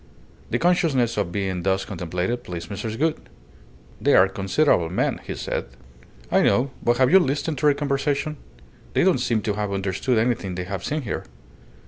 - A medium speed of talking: Yes, average, 175 wpm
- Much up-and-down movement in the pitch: Yes, wide, 6.5 semitones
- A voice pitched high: No, low, 110 Hz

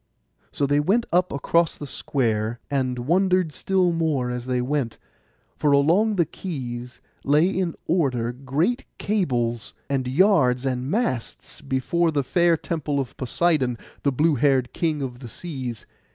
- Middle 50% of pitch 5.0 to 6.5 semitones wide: Yes, average, 5.3 semitones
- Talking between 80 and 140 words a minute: No, average, 150 wpm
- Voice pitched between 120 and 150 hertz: Yes, medium, 140 Hz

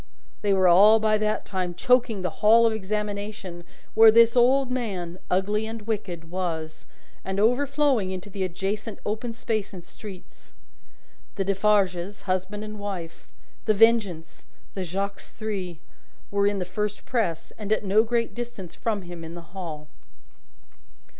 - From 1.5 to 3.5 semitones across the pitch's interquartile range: Yes, average, 3.1 semitones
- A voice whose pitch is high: Yes, high, 205 Hz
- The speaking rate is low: No, average, 150 wpm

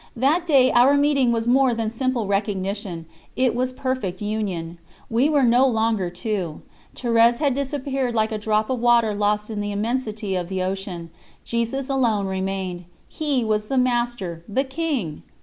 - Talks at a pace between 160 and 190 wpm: Yes, average, 165 wpm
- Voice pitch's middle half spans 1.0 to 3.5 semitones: No, average, 4.4 semitones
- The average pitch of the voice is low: No, high, 230 Hz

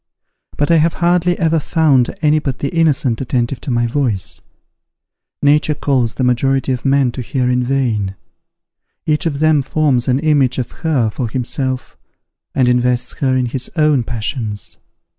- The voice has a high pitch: No, low, 135 Hz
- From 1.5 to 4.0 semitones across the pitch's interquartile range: Yes, average, 3.5 semitones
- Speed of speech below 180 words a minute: Yes, average, 160 wpm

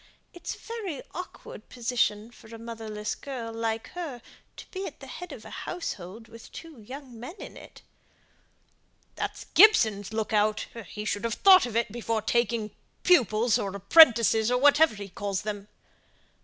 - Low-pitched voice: No, high, 230 Hz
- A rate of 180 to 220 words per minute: No, average, 165 wpm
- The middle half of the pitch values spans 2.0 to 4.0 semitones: No, average, 4.5 semitones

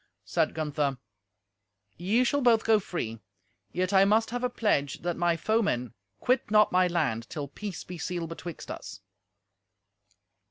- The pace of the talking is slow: No, average, 150 wpm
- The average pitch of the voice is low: No, medium, 180 Hz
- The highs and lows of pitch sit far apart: Yes, wide, 6.3 semitones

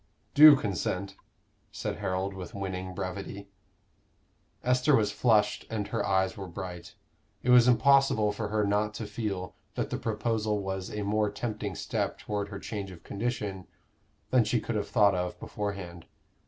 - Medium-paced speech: Yes, average, 155 wpm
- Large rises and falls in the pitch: No, narrow, 2.4 semitones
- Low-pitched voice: Yes, low, 105 Hz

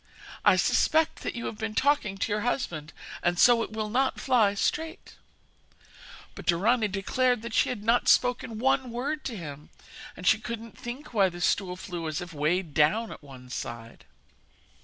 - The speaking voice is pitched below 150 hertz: No, high, 215 Hz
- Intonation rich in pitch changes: Yes, wide, 5.8 semitones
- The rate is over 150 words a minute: Yes, average, 180 wpm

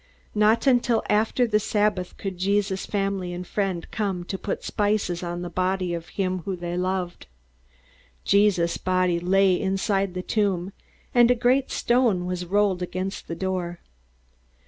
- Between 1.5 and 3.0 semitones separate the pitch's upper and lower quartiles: Yes, narrow, 2.6 semitones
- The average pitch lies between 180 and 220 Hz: Yes, high, 190 Hz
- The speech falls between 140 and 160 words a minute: Yes, average, 155 wpm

